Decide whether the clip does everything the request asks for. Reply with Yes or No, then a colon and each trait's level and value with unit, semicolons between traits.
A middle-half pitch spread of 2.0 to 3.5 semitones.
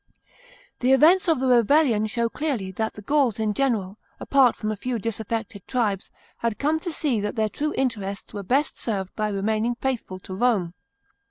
No: average, 4.3 semitones